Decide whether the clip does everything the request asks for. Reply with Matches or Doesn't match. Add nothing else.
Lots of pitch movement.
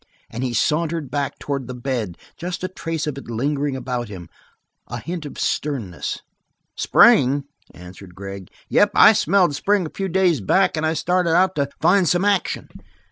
Matches